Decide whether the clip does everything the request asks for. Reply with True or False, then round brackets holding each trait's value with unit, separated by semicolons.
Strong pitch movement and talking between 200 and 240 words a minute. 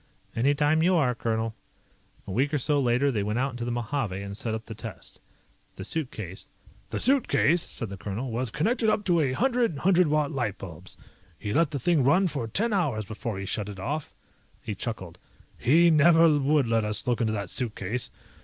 True (6.2 semitones; 205 wpm)